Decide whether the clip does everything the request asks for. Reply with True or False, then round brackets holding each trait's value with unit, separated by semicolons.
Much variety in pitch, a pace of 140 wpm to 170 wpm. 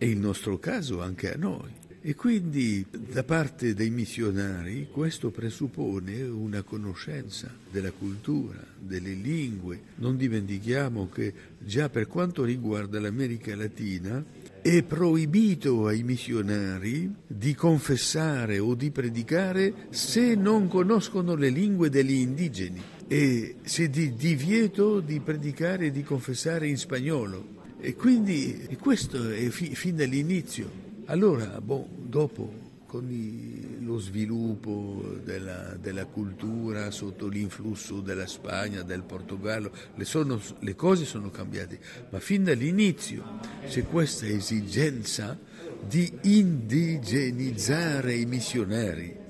False (7.2 semitones; 120 wpm)